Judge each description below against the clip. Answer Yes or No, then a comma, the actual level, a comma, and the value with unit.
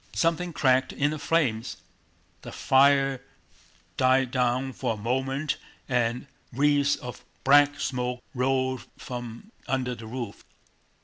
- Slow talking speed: Yes, slow, 120 wpm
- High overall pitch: No, low, 130 Hz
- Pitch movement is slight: Yes, narrow, 2.3 semitones